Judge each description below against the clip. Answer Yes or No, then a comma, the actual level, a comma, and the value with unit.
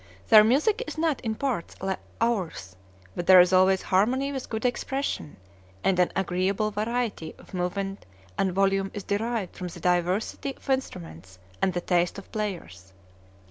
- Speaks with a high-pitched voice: Yes, high, 195 Hz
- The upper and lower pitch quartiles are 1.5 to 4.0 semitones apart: No, average, 4.4 semitones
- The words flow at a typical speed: Yes, average, 165 wpm